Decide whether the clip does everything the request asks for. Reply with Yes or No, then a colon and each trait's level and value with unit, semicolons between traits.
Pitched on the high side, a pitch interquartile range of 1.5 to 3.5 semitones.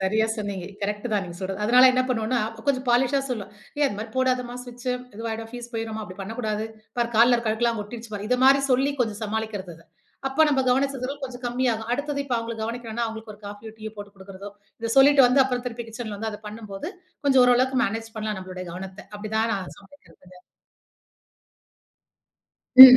Yes: high, 225 Hz; average, 3.2 semitones